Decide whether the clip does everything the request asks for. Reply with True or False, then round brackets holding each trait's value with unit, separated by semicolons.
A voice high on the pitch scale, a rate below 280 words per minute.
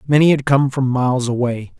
False (130 Hz; 200 wpm)